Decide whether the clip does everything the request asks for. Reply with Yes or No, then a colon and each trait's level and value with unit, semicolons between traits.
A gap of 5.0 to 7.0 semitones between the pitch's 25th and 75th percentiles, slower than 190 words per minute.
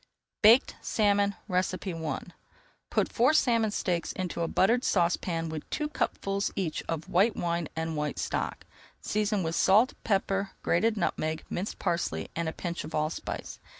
No: average, 4.0 semitones; average, 150 wpm